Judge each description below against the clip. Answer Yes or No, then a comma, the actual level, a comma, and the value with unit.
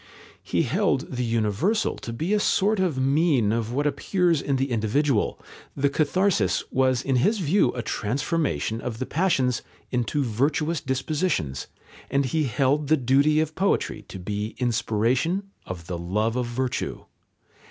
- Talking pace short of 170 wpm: Yes, average, 150 wpm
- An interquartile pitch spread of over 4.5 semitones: Yes, average, 5.3 semitones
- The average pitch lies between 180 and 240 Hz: No, low, 130 Hz